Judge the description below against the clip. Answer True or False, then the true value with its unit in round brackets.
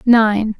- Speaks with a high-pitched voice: True (220 Hz)